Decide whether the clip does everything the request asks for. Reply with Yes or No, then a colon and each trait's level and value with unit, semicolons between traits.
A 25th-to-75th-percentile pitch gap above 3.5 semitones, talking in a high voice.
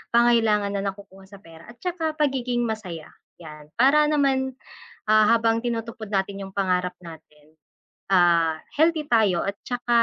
Yes: average, 5.0 semitones; high, 215 Hz